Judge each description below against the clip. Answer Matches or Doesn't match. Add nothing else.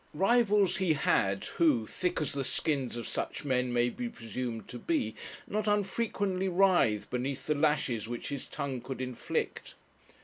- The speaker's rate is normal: Matches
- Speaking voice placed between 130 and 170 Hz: Matches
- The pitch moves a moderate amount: Doesn't match